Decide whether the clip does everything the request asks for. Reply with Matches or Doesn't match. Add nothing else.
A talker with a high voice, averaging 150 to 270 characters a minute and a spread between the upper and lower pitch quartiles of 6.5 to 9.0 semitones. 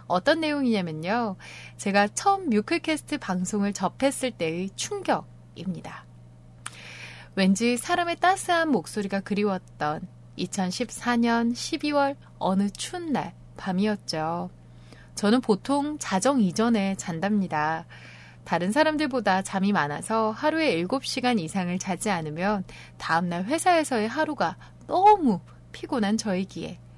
Matches